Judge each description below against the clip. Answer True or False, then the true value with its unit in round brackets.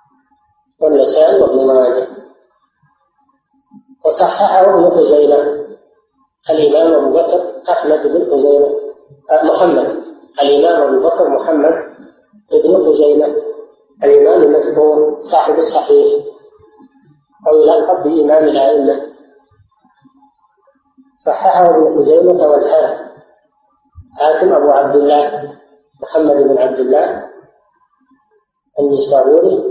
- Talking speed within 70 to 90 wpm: True (80 wpm)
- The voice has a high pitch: True (210 Hz)